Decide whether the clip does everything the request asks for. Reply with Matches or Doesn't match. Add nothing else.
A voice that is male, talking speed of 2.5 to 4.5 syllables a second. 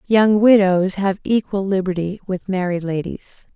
Doesn't match